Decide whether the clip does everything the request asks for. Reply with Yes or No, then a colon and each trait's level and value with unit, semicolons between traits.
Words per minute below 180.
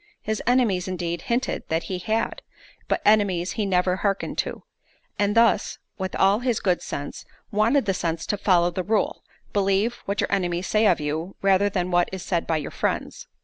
No: average, 190 wpm